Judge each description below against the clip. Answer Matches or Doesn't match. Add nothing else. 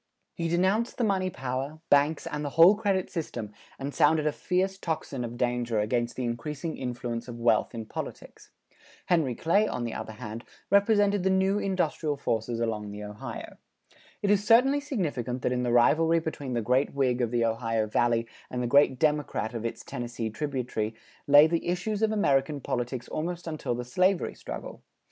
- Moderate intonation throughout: Doesn't match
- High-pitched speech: Doesn't match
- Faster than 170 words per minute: Matches